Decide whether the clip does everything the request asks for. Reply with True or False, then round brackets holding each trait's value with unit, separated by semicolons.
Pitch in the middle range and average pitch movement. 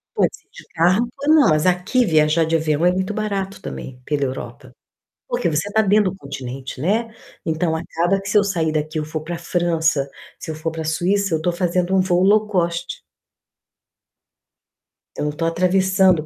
True (175 Hz; 3.5 semitones)